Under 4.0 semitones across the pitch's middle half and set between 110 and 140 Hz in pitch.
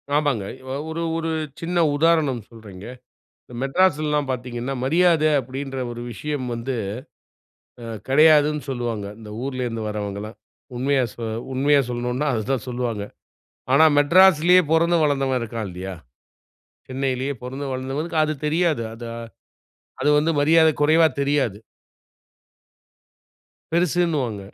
No: average, 4.3 semitones; low, 135 Hz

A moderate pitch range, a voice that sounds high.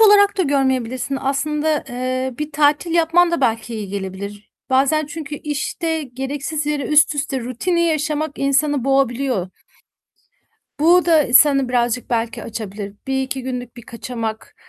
Yes: average, 3.9 semitones; very high, 275 Hz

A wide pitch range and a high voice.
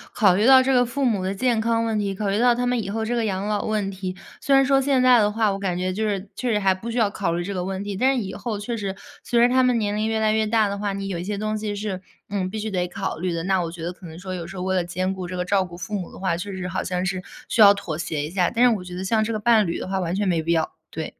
No: average, 3.2 semitones; high, 200 Hz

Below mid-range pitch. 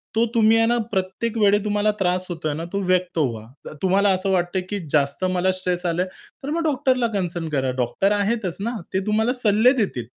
No: high, 190 Hz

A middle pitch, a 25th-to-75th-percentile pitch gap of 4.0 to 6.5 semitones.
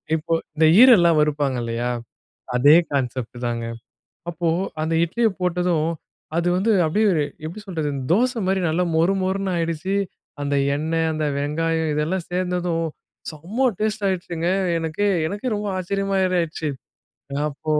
No: medium, 165 Hz; average, 3.6 semitones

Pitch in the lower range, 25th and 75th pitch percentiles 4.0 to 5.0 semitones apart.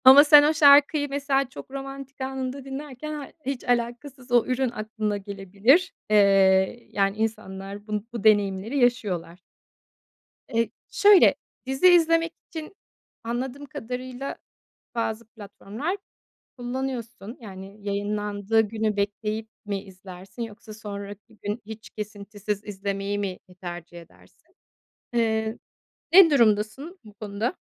No: high, 225 Hz; average, 4.7 semitones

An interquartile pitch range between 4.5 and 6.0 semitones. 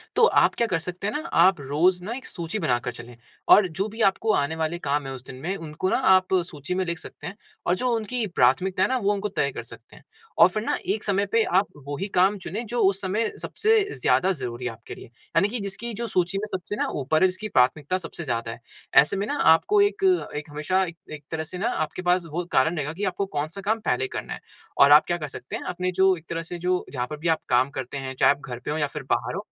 Yes: average, 5.2 semitones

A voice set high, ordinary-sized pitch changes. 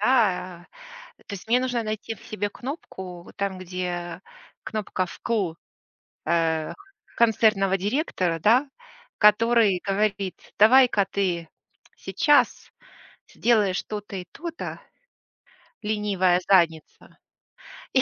Yes: high, 200 Hz; average, 3.7 semitones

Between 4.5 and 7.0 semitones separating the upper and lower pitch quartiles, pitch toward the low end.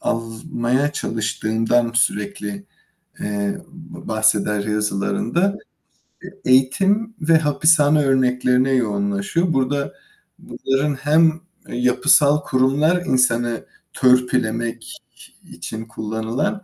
Yes: average, 4.9 semitones; low, 125 Hz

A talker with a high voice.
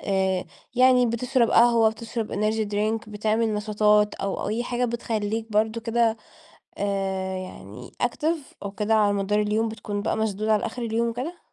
Yes: high, 220 Hz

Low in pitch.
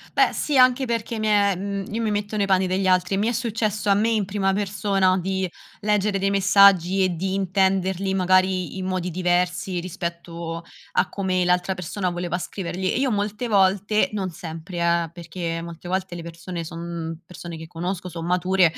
No: medium, 185 Hz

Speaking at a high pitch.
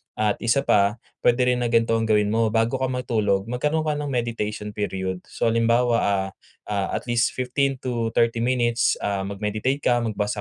No: low, 115 Hz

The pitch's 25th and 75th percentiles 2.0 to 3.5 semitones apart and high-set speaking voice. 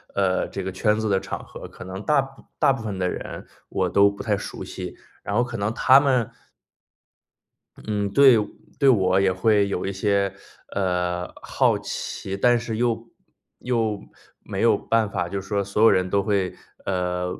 No: average, 3.2 semitones; low, 100 Hz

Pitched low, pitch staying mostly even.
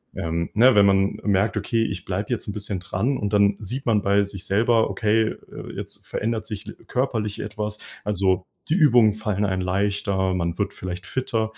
Yes: low, 105 Hz; narrow, 2.3 semitones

